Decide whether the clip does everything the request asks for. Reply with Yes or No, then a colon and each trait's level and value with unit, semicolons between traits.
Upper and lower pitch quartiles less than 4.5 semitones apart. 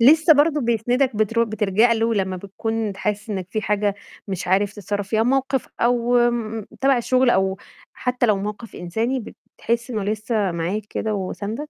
Yes: average, 3.1 semitones